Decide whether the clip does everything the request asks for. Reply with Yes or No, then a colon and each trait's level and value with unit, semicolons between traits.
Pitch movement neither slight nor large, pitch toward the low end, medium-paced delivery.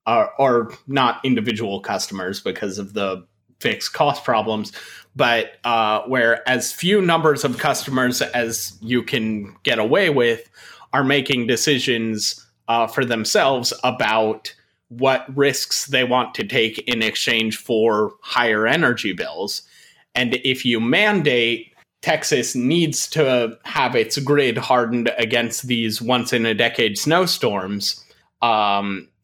No: average, 3.7 semitones; low, 125 Hz; slow, 130 wpm